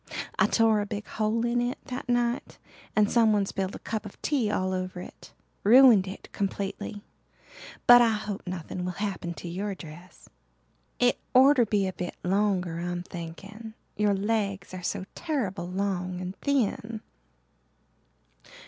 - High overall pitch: Yes, high, 205 Hz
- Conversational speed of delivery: Yes, average, 155 wpm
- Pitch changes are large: No, average, 3.6 semitones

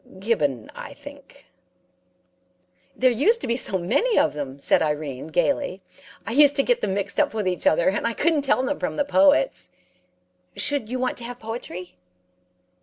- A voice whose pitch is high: Yes, high, 235 Hz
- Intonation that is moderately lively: No, wide, 7.9 semitones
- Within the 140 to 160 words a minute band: No, average, 180 wpm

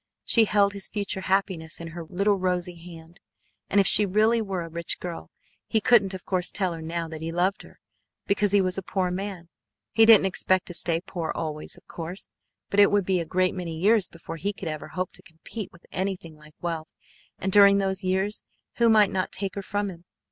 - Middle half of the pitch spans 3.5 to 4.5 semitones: No, average, 2.9 semitones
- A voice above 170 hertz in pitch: Yes, medium, 185 Hz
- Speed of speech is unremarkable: No, fast, 220 wpm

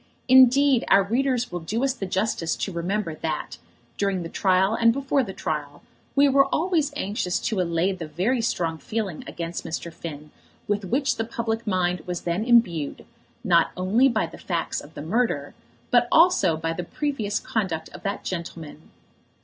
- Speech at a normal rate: Yes, average, 175 wpm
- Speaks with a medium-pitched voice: No, high, 195 Hz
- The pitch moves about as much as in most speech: No, wide, 6.0 semitones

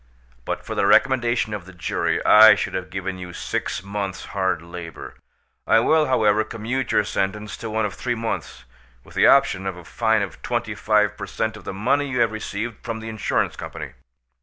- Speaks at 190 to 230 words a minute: Yes, average, 200 wpm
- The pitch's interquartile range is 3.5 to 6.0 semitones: No, average, 2.8 semitones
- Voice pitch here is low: Yes, low, 105 Hz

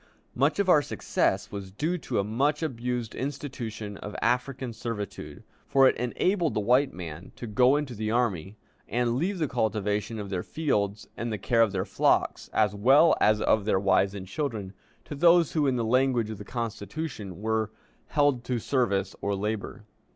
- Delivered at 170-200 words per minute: Yes, average, 180 wpm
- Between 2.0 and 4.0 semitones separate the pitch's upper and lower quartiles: No, average, 4.8 semitones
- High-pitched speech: No, low, 115 Hz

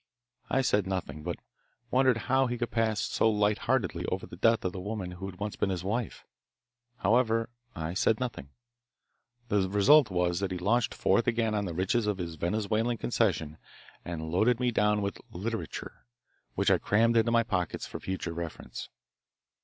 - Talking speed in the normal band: Yes, average, 170 wpm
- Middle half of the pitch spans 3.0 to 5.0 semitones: Yes, average, 4.1 semitones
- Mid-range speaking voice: No, low, 105 Hz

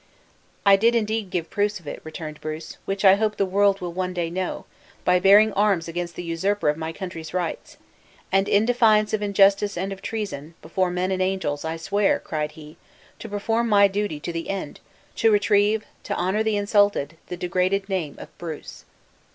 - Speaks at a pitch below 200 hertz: Yes, high, 190 Hz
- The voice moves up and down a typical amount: Yes, average, 3.4 semitones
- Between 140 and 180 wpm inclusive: No, average, 190 wpm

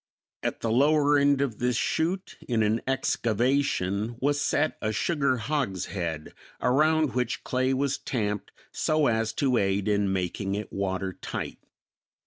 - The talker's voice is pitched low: Yes, low, 120 Hz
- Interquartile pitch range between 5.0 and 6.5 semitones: Yes, wide, 5.5 semitones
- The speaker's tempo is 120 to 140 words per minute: Yes, slow, 135 wpm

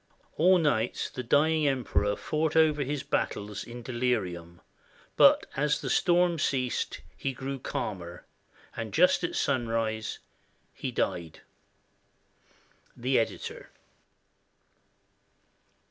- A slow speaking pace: Yes, slow, 100 wpm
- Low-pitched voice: Yes, low, 125 Hz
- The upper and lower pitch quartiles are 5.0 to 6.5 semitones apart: Yes, average, 5.3 semitones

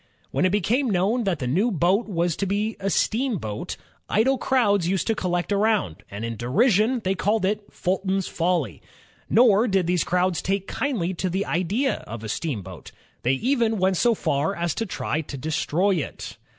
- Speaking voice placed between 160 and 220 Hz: Yes, high, 190 Hz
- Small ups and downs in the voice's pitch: No, average, 4.4 semitones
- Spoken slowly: No, average, 180 wpm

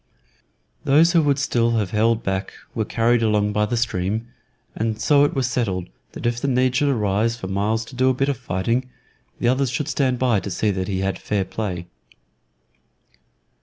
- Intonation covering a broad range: No, average, 3.7 semitones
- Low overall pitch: Yes, low, 115 Hz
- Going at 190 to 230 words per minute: Yes, average, 195 wpm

